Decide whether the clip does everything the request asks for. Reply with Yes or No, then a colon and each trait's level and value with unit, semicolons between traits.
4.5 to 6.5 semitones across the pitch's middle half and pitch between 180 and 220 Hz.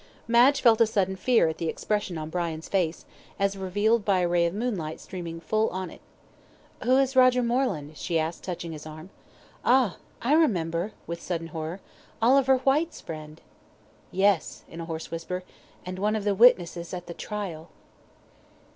Yes: wide, 5.5 semitones; medium, 185 Hz